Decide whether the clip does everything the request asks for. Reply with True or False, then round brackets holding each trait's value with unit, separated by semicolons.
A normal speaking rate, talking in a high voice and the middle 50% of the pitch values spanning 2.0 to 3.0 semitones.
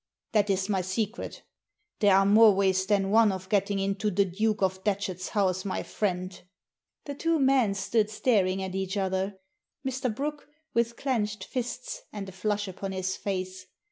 True (170 wpm; 200 Hz; 2.6 semitones)